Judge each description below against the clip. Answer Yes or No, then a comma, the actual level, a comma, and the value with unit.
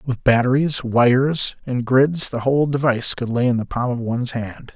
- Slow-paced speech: No, average, 200 wpm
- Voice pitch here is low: Yes, low, 125 Hz